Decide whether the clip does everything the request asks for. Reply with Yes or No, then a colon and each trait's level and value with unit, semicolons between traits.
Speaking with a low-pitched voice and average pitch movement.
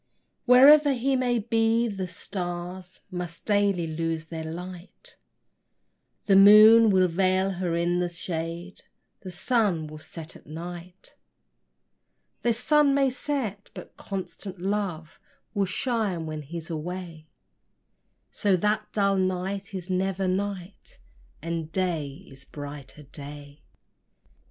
No: medium, 185 Hz; average, 3.6 semitones